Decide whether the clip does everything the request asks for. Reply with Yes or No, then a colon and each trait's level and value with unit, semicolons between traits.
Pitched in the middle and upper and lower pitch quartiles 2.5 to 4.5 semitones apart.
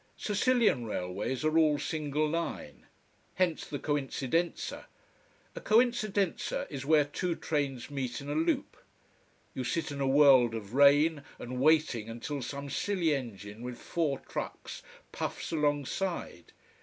Yes: medium, 145 Hz; average, 4.0 semitones